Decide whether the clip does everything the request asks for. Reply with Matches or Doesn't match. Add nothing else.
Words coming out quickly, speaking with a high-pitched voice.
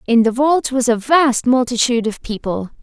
Doesn't match